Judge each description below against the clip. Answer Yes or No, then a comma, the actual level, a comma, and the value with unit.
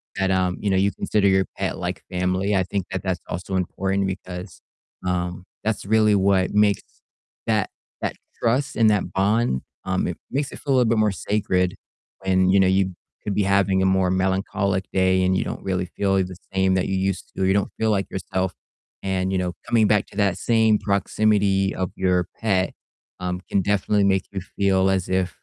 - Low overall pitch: Yes, very low, 95 Hz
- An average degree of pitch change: No, narrow, 1.5 semitones